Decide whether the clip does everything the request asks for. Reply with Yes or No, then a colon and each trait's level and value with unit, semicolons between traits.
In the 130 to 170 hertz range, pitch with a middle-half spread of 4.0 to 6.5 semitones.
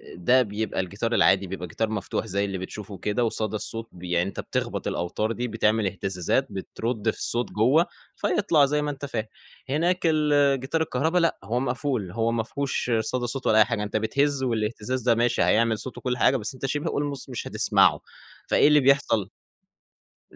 No: low, 115 Hz; average, 4.4 semitones